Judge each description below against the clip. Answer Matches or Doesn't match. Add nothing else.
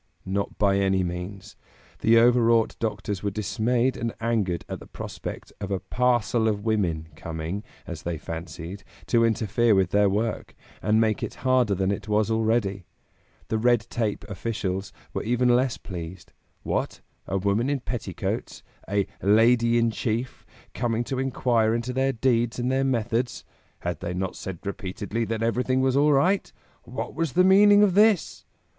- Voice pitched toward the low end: Matches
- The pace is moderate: Matches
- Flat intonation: Doesn't match